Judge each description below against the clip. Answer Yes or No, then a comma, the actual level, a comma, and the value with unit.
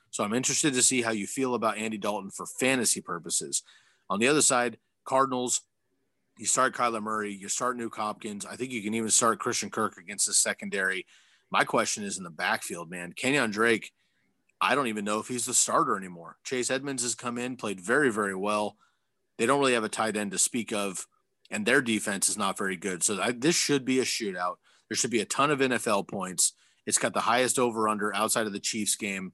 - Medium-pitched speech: No, low, 115 Hz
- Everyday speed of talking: No, fast, 220 wpm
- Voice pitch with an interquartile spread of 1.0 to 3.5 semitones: Yes, average, 3.0 semitones